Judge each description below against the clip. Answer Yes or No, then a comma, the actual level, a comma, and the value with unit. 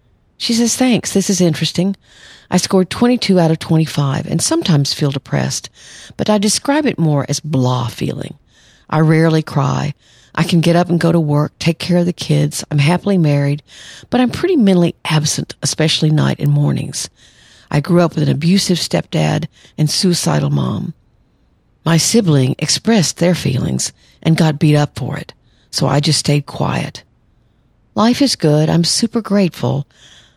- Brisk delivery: No, average, 165 wpm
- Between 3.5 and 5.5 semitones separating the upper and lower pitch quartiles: Yes, average, 3.8 semitones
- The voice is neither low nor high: Yes, medium, 155 Hz